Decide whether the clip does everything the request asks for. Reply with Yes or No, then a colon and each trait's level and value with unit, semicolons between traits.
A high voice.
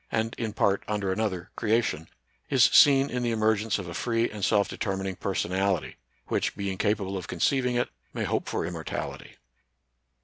No: low, 105 Hz